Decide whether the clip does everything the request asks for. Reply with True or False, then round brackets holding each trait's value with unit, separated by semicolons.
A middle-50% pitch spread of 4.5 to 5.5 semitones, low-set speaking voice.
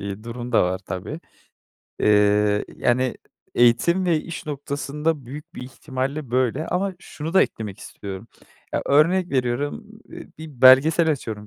True (5.2 semitones; 130 Hz)